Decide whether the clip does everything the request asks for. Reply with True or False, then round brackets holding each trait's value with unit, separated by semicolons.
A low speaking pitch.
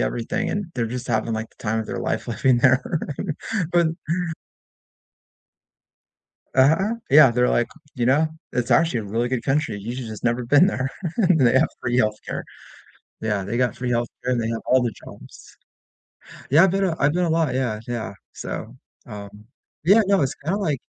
True (125 Hz)